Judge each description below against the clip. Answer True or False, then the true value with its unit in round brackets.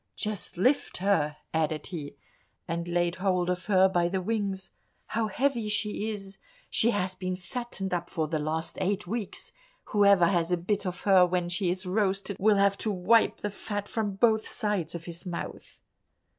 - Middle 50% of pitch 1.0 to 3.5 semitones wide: True (2.9 semitones)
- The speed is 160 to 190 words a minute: True (175 wpm)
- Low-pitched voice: False (190 Hz)